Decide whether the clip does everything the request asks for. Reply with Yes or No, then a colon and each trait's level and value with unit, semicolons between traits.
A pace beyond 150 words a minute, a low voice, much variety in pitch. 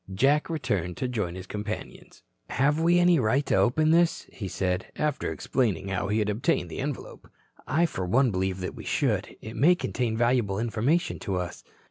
Yes: average, 185 wpm; low, 115 Hz; wide, 7.1 semitones